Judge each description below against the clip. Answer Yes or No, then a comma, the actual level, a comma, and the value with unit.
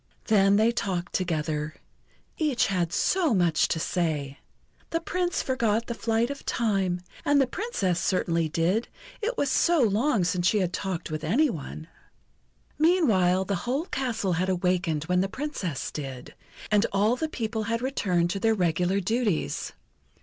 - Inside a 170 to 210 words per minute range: No, average, 155 wpm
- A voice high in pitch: Yes, high, 195 Hz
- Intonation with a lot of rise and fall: Yes, wide, 5.7 semitones